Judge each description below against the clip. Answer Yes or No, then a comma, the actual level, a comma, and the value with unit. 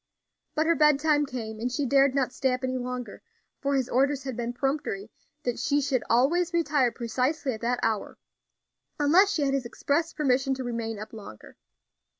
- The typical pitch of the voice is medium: No, very high, 265 Hz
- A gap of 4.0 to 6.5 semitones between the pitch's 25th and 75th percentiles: No, average, 3.2 semitones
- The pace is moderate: Yes, average, 180 wpm